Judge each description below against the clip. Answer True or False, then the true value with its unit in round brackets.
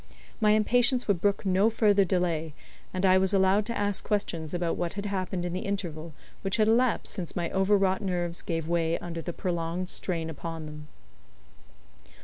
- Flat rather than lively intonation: False (3.3 semitones)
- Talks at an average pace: True (180 wpm)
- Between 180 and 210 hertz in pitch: True (185 Hz)